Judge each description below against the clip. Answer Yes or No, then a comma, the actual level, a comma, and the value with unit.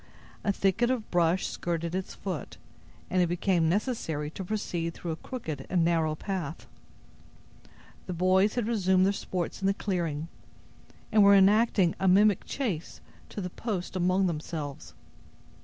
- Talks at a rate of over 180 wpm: No, average, 150 wpm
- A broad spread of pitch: No, average, 3.2 semitones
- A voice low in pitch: No, medium, 185 Hz